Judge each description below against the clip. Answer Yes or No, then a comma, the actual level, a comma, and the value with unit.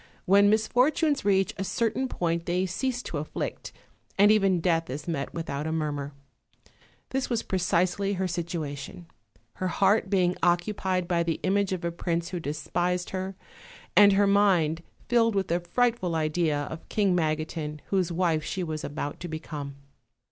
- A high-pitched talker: No, medium, 180 Hz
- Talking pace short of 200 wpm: Yes, average, 160 wpm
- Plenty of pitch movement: No, average, 3.4 semitones